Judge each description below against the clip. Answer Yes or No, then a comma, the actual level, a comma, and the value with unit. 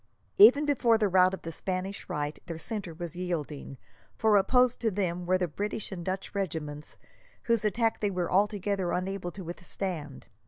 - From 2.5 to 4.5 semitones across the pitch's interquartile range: Yes, average, 3.3 semitones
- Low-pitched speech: No, medium, 185 Hz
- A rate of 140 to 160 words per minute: No, average, 170 wpm